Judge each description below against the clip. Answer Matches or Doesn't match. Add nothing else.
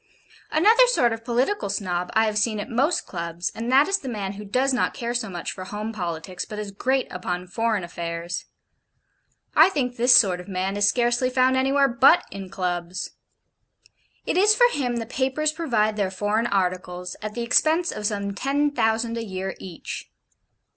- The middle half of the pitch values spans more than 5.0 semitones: Matches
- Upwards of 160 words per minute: Matches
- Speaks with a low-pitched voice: Doesn't match